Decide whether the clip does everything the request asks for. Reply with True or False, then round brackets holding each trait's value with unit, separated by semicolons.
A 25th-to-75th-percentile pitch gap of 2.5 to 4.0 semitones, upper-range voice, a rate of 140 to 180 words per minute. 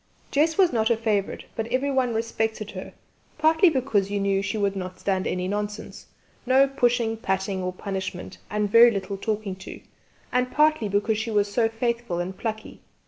True (3.5 semitones; 220 Hz; 175 wpm)